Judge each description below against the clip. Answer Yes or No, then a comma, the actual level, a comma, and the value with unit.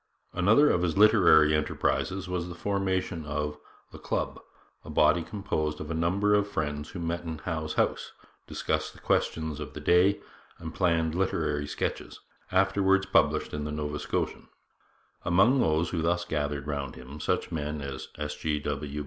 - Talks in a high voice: No, very low, 80 Hz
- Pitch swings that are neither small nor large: Yes, average, 3.6 semitones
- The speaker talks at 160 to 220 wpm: Yes, average, 165 wpm